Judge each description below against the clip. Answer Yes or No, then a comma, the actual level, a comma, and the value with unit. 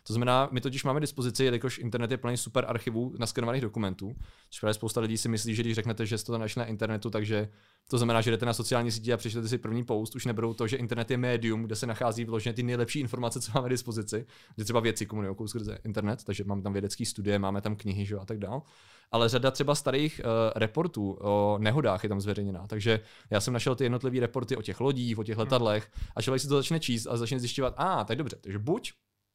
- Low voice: Yes, low, 115 Hz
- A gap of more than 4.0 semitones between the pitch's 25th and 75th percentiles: No, average, 2.7 semitones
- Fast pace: Yes, fast, 235 wpm